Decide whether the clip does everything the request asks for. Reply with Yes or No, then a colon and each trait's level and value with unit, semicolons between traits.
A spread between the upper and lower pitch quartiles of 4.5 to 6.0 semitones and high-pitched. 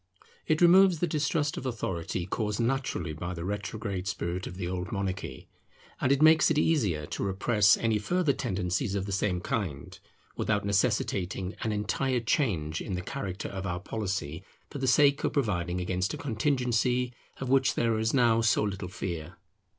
No: wide, 5.5 semitones; low, 105 Hz